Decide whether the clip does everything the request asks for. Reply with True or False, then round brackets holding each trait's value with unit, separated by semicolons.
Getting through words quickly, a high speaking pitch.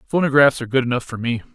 False (235 wpm; 130 Hz)